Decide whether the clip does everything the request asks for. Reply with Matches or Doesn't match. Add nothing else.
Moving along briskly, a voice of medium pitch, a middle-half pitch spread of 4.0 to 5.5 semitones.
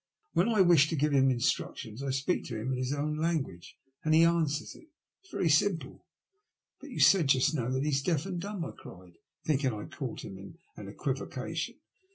Matches